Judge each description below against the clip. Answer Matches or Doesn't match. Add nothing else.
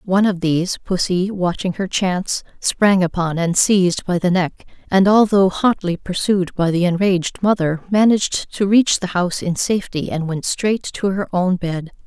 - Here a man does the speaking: Doesn't match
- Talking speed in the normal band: Matches